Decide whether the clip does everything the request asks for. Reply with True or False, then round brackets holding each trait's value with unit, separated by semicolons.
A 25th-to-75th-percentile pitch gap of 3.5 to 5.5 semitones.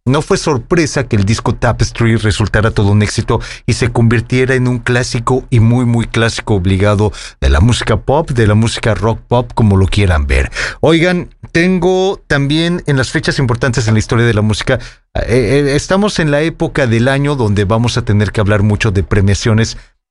True (4.2 semitones)